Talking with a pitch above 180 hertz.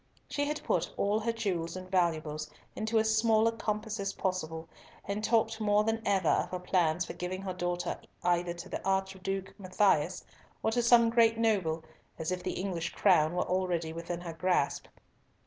Yes: high, 190 Hz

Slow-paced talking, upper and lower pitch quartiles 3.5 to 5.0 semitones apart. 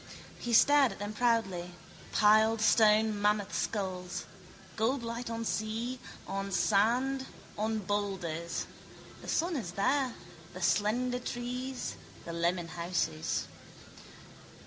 Yes: slow, 110 wpm; average, 4.0 semitones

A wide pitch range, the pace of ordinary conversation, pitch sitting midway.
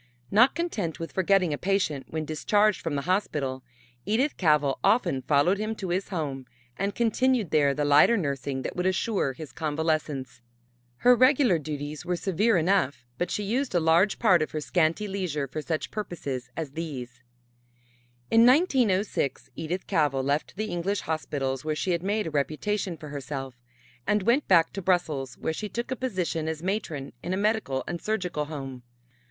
Yes: wide, 5.7 semitones; average, 175 wpm; medium, 165 Hz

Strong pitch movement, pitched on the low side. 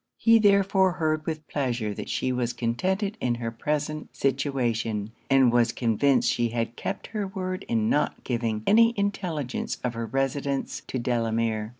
Yes: wide, 6.2 semitones; low, 130 Hz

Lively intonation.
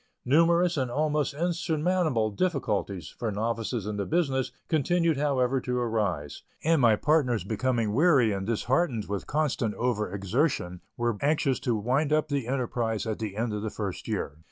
Yes: wide, 5.9 semitones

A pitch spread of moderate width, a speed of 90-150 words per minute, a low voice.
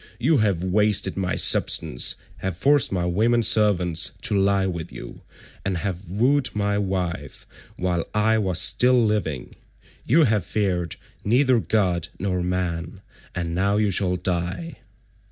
Yes: average, 3.3 semitones; average, 140 wpm; very low, 95 Hz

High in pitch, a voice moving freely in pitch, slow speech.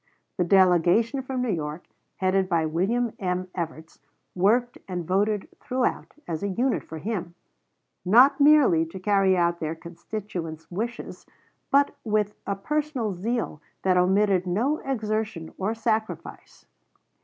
No: high, 195 Hz; average, 4.7 semitones; slow, 130 wpm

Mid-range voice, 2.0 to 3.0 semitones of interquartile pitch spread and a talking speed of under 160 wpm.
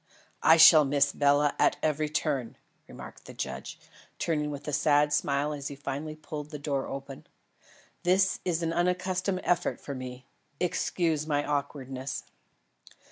Yes: medium, 150 Hz; narrow, 2.5 semitones; average, 145 wpm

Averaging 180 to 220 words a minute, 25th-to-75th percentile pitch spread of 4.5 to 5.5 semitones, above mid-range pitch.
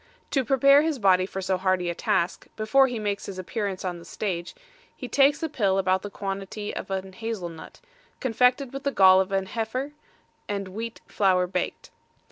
Yes: average, 190 wpm; average, 4.8 semitones; high, 200 Hz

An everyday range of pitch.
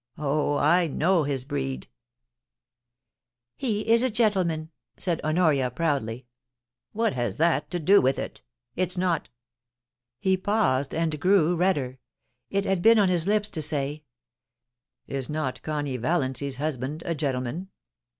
No: wide, 5.8 semitones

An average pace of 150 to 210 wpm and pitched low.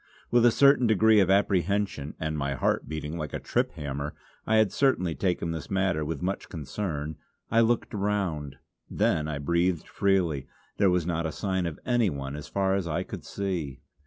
Yes: average, 185 wpm; very low, 90 Hz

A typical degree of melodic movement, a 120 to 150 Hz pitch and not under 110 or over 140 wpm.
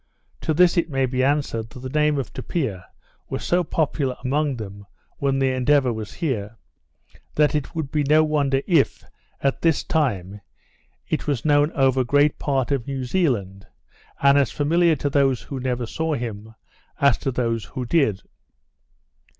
No: average, 3.6 semitones; low, 135 Hz; average, 165 wpm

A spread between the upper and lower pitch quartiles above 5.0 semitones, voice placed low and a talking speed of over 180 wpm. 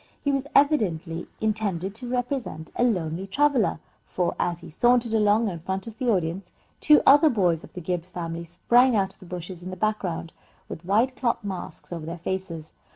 No: wide, 5.6 semitones; high, 190 Hz; average, 190 wpm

